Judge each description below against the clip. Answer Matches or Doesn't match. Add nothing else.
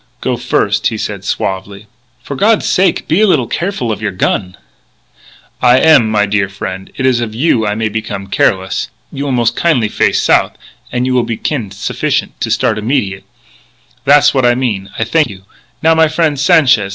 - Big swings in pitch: Matches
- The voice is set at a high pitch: Doesn't match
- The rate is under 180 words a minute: Doesn't match